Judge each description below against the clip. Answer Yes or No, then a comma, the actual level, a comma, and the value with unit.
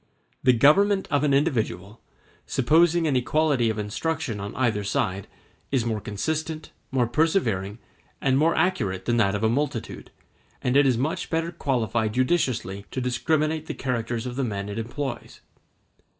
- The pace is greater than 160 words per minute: No, average, 155 wpm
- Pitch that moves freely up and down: Yes, wide, 5.7 semitones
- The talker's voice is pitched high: No, low, 125 Hz